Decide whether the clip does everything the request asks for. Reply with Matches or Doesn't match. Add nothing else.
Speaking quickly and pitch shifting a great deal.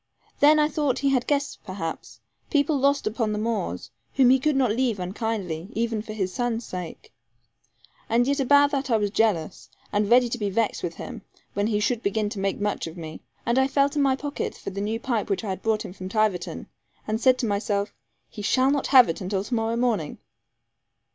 Doesn't match